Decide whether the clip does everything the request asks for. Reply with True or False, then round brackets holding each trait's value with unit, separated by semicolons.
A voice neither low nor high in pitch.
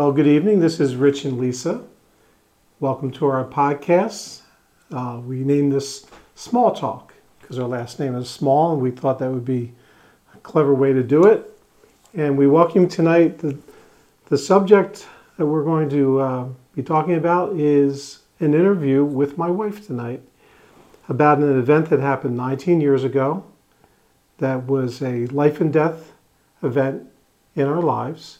True (145 Hz)